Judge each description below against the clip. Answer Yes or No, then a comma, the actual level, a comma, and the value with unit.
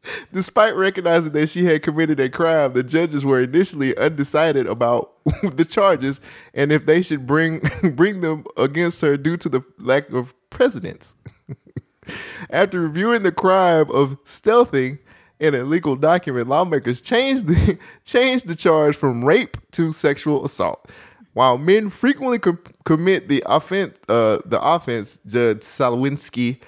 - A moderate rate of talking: Yes, average, 145 wpm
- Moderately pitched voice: Yes, medium, 155 Hz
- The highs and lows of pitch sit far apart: No, average, 4.8 semitones